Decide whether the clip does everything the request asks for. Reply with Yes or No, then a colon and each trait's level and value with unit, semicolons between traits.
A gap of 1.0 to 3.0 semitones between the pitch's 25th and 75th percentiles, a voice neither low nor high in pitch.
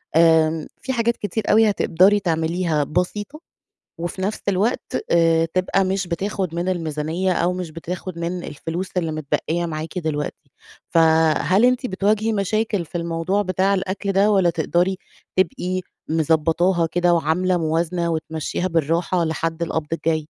Yes: average, 2.7 semitones; medium, 175 Hz